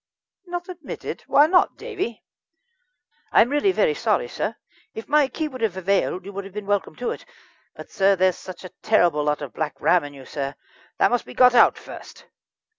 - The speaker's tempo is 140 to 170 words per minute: No, average, 200 wpm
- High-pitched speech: Yes, high, 205 Hz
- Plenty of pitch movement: Yes, wide, 8.5 semitones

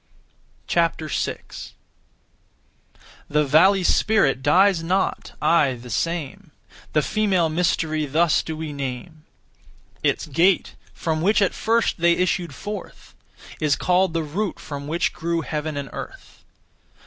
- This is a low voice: No, medium, 165 Hz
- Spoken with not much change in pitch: No, average, 3.3 semitones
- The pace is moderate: No, slow, 125 wpm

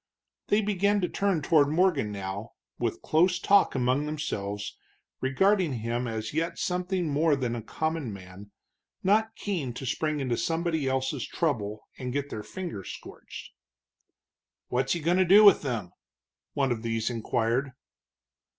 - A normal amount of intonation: No, wide, 7.0 semitones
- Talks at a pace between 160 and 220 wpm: No, average, 150 wpm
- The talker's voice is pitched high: No, medium, 140 Hz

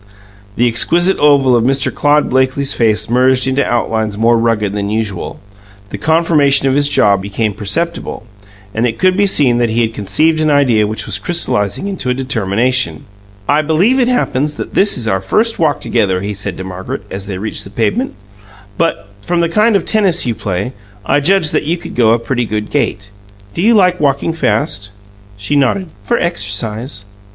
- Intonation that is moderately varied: No, wide, 7.0 semitones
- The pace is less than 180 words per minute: No, average, 190 wpm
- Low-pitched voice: Yes, low, 125 Hz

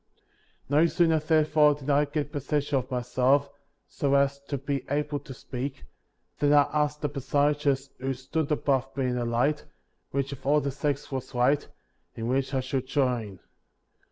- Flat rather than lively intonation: Yes, narrow, 2.0 semitones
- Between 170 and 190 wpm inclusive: Yes, average, 175 wpm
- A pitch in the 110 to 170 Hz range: Yes, medium, 140 Hz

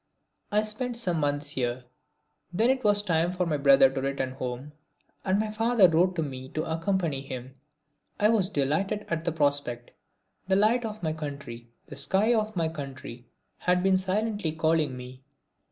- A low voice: No, medium, 165 Hz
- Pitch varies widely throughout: Yes, wide, 6.8 semitones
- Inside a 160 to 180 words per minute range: Yes, average, 170 wpm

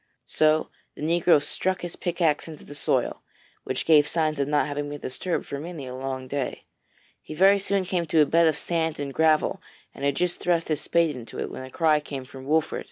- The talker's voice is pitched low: No, medium, 155 Hz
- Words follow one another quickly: Yes, fast, 220 wpm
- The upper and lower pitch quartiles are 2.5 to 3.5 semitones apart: Yes, average, 2.9 semitones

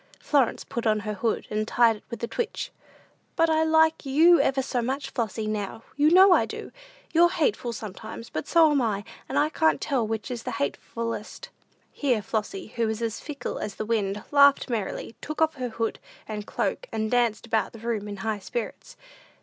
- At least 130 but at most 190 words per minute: No, average, 200 wpm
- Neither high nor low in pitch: No, high, 235 Hz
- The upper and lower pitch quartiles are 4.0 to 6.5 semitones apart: Yes, average, 4.9 semitones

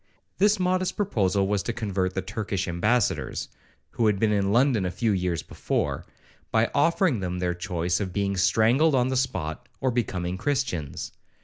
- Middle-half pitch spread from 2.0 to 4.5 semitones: No, average, 5.2 semitones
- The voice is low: Yes, low, 100 Hz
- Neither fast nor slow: Yes, average, 170 wpm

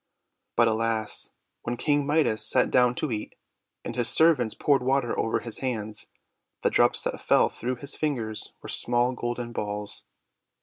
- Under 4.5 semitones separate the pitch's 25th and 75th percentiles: Yes, average, 3.1 semitones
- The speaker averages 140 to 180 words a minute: Yes, average, 160 wpm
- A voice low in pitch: Yes, low, 120 Hz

